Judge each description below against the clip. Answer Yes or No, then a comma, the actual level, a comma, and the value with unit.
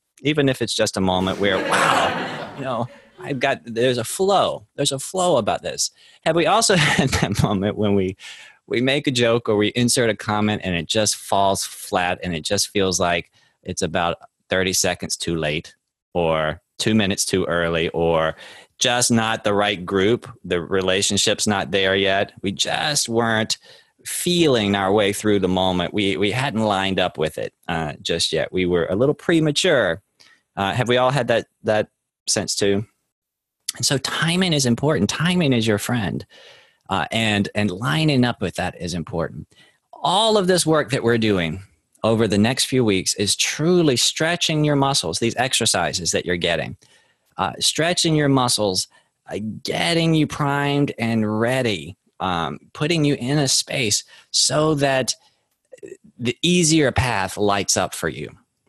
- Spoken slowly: No, average, 170 wpm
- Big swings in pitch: Yes, wide, 6.4 semitones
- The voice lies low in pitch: Yes, low, 110 Hz